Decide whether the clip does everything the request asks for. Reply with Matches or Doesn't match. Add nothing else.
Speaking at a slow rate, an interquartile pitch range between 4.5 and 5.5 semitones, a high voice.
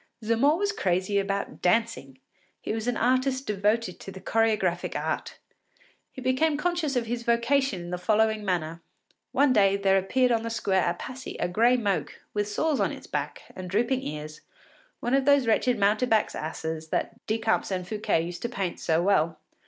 Doesn't match